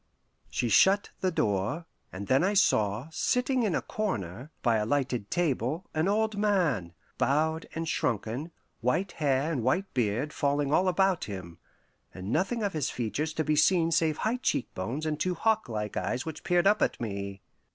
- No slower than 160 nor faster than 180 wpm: Yes, average, 175 wpm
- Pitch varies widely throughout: Yes, wide, 8.0 semitones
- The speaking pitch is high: No, medium, 150 Hz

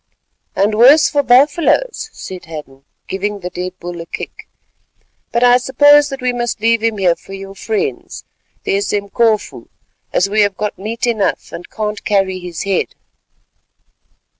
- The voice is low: No, high, 210 Hz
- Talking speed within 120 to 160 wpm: Yes, average, 155 wpm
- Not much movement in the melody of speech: No, average, 4.4 semitones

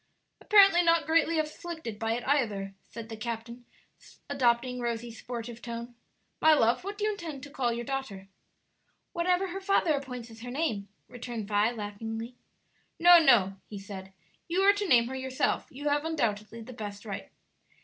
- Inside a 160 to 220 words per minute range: Yes, average, 170 wpm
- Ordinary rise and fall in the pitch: No, wide, 5.9 semitones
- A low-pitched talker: No, high, 245 Hz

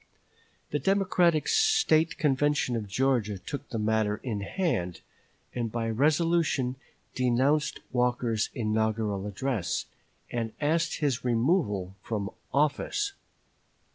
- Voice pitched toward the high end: No, low, 125 Hz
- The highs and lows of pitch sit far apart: Yes, wide, 5.7 semitones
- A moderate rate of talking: No, slow, 105 wpm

